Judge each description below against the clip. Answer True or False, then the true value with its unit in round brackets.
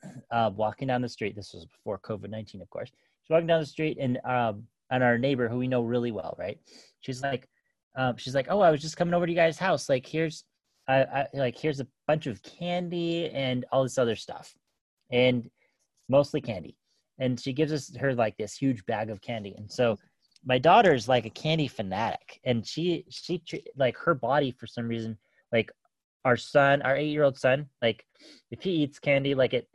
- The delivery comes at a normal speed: False (210 wpm)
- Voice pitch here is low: True (130 Hz)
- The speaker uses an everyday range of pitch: True (4.4 semitones)